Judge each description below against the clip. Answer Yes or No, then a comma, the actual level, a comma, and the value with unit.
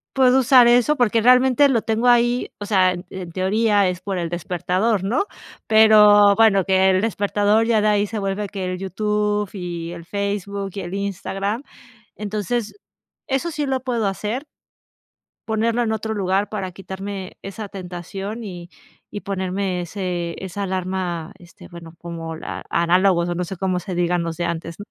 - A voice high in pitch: Yes, high, 200 Hz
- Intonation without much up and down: No, average, 3.2 semitones